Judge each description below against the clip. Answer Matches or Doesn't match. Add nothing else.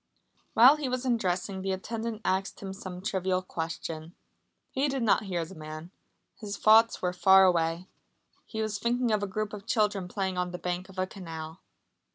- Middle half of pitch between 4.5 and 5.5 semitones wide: Doesn't match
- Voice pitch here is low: Doesn't match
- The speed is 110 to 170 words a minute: Doesn't match